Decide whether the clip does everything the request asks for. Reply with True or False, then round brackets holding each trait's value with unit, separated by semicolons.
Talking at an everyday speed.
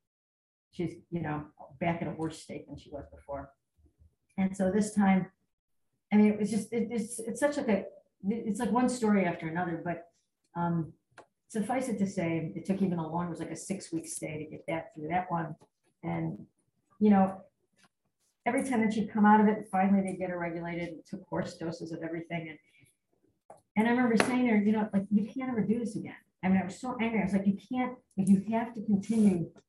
False (220 wpm)